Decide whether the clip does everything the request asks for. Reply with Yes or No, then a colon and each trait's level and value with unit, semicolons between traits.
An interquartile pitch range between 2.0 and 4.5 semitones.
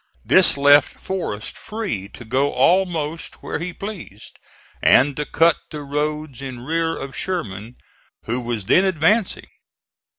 No: wide, 5.4 semitones